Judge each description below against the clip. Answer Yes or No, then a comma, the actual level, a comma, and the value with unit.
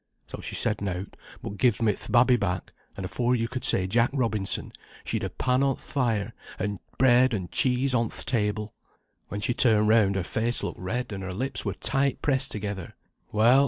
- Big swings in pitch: No, average, 3.7 semitones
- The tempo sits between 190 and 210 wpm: Yes, average, 200 wpm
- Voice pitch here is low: Yes, low, 110 Hz